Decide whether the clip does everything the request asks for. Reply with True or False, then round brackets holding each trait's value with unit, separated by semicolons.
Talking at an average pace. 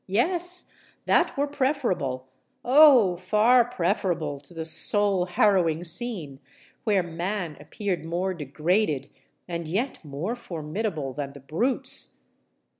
False (105 wpm)